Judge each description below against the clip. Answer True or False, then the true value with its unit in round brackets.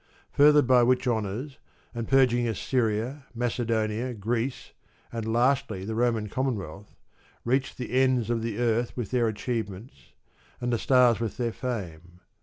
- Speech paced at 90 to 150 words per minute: True (140 wpm)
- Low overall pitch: True (120 Hz)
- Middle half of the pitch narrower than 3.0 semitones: True (2.5 semitones)